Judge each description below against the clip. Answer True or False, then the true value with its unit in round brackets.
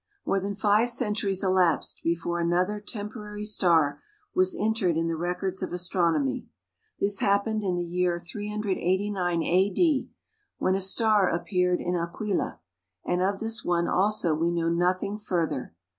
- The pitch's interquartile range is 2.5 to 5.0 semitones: True (3.2 semitones)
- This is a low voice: False (185 Hz)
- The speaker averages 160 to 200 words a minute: False (145 wpm)